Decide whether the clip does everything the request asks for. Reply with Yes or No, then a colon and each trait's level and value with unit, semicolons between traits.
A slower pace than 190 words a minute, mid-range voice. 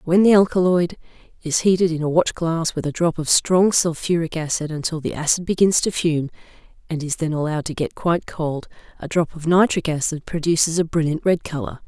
No: average, 195 wpm; medium, 165 Hz